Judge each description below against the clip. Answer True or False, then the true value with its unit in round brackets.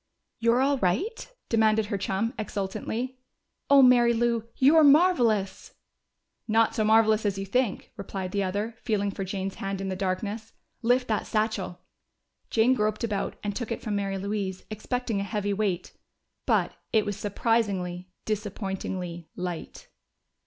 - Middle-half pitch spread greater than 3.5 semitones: False (3.0 semitones)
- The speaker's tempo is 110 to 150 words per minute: True (145 wpm)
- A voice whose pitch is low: False (210 Hz)